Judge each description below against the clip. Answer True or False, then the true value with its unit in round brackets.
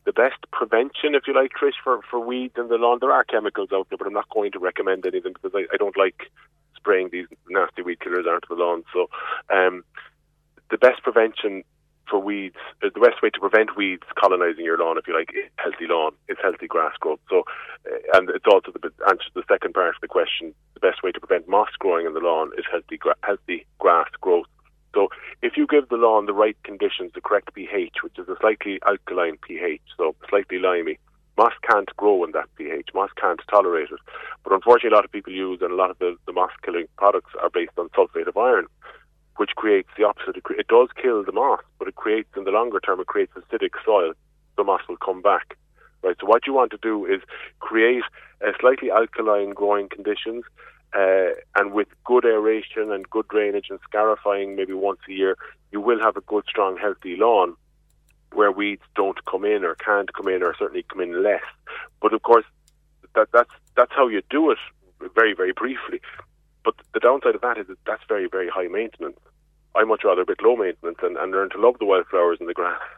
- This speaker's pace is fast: True (215 wpm)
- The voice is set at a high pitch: True (395 Hz)